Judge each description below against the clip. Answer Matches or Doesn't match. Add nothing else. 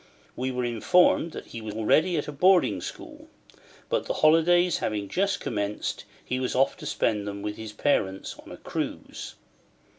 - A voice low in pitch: Matches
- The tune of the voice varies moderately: Doesn't match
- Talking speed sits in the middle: Matches